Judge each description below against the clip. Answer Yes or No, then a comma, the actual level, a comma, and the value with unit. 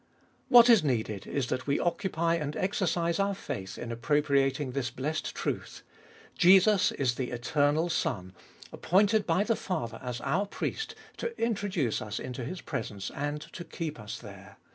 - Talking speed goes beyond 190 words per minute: No, average, 165 wpm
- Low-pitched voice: No, medium, 150 Hz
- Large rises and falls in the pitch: Yes, wide, 6.8 semitones